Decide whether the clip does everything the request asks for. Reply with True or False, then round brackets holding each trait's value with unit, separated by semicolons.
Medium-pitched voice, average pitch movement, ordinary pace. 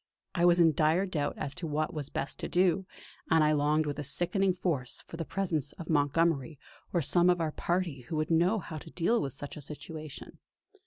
False (160 Hz; 3.0 semitones; 215 wpm)